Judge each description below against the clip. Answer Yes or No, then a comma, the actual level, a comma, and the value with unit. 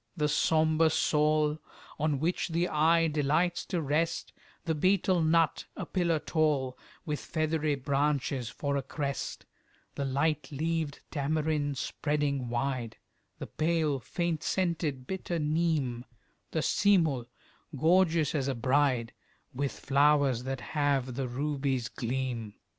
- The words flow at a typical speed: No, slow, 125 wpm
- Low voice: No, medium, 150 Hz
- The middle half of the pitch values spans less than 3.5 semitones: Yes, average, 3.0 semitones